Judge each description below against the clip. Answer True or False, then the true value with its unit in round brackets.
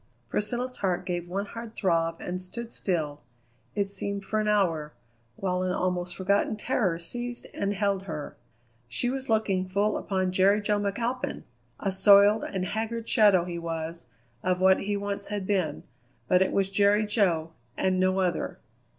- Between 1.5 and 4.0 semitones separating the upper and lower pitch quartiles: True (2.5 semitones)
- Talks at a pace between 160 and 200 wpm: True (165 wpm)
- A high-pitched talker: True (195 Hz)